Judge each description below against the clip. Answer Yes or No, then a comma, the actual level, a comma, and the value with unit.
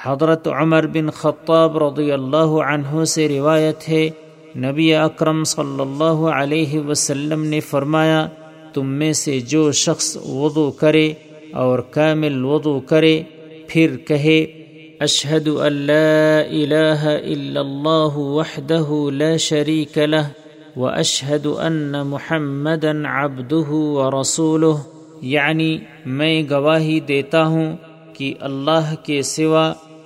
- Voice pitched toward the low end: No, medium, 155 Hz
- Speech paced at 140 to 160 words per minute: No, slow, 110 wpm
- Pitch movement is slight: Yes, narrow, 1.3 semitones